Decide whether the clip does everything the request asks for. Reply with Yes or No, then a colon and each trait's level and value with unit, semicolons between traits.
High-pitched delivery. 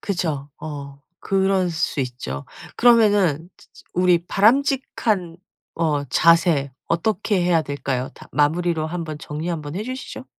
No: medium, 170 Hz